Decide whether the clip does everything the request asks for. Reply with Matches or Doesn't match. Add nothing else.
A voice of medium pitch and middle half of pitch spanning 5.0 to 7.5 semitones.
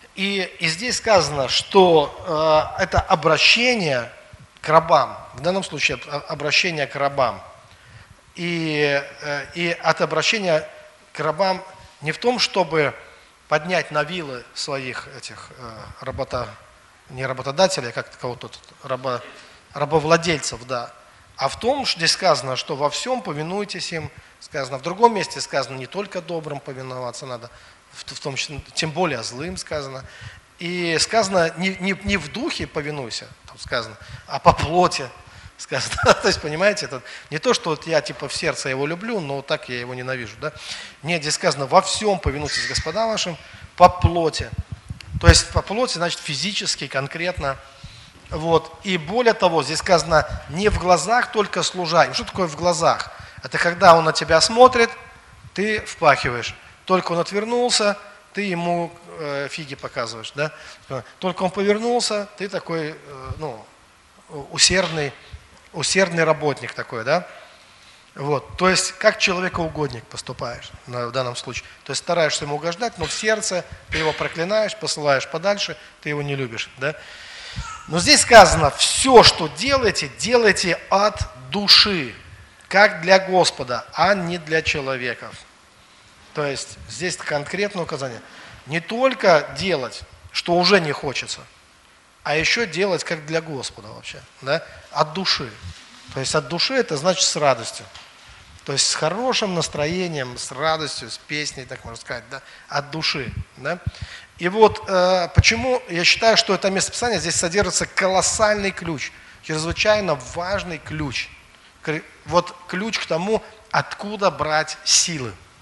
Matches